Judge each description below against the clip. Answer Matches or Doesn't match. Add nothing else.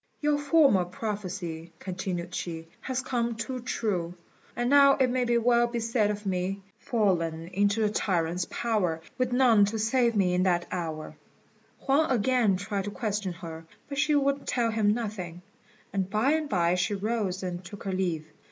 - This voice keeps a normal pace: Matches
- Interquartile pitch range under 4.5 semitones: Doesn't match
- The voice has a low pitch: Doesn't match